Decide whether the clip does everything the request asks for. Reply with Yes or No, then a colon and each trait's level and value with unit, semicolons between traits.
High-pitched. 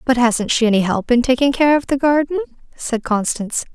Yes: high, 245 Hz